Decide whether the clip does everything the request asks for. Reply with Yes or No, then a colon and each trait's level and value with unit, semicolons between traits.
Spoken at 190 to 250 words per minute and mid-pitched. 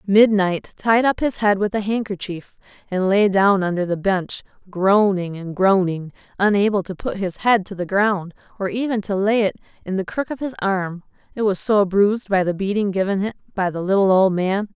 No: fast, 205 wpm; high, 195 Hz